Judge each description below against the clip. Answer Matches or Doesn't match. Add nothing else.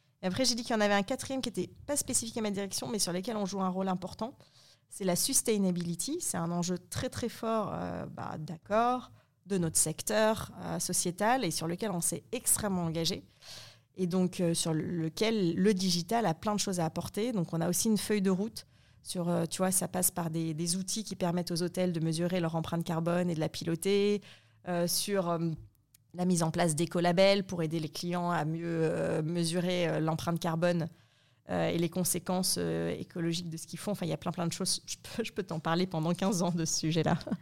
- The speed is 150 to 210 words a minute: Doesn't match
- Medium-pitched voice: Matches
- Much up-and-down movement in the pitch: Doesn't match